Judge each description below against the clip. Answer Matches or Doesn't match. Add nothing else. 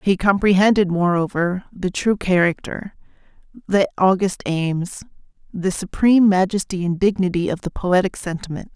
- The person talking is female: Matches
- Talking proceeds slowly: Matches